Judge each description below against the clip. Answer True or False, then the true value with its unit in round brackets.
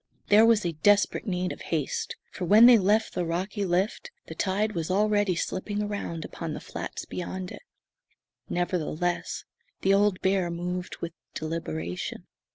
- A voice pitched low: False (185 Hz)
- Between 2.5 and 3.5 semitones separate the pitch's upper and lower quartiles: True (3.2 semitones)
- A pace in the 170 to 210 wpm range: False (150 wpm)